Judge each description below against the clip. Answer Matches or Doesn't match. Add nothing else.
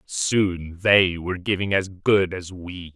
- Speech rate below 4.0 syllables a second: Matches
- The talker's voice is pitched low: Matches